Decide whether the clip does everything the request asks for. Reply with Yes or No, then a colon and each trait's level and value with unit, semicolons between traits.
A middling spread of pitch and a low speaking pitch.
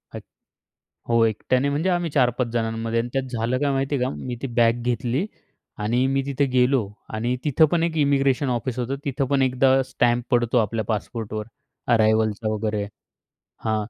Yes: average, 3.1 semitones; low, 125 Hz